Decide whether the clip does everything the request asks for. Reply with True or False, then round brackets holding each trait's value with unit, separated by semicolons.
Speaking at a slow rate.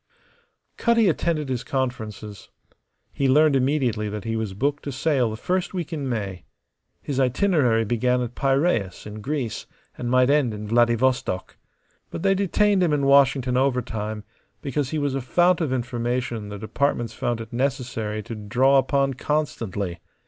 False (155 wpm)